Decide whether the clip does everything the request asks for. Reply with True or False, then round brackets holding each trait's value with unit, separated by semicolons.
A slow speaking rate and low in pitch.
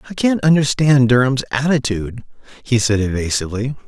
True (125 wpm; 130 Hz)